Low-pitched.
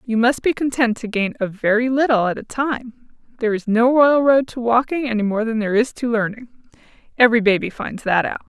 No: high, 235 Hz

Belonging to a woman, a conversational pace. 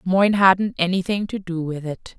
Yes: female; average, 190 wpm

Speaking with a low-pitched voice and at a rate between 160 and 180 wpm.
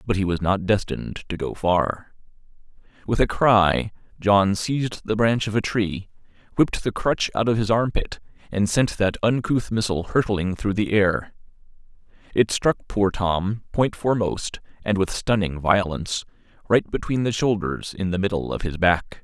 Yes: low, 100 Hz; average, 170 wpm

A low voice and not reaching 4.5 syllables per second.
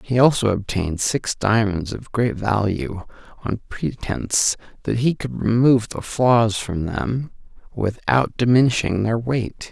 Yes: low, 110 Hz; 4.1 syllables/s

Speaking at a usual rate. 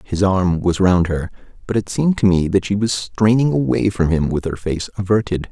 No: fast, 230 wpm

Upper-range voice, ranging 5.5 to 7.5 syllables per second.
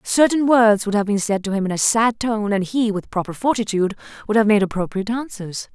Yes: high, 210 Hz; 5.9 syllables/s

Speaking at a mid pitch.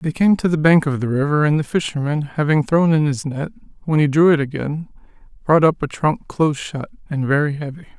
Yes: medium, 150 Hz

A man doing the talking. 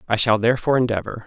Yes: male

